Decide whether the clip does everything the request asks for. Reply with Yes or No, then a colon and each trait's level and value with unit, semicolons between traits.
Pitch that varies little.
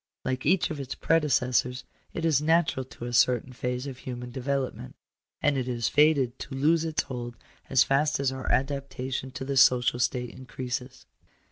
Yes: narrow, 2.2 semitones